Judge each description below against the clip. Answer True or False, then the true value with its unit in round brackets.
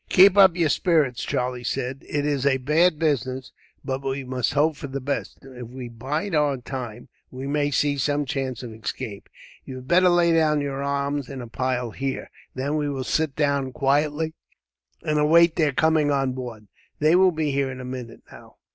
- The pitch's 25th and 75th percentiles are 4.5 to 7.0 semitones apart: False (2.9 semitones)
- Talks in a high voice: False (140 Hz)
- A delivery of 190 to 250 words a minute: True (195 wpm)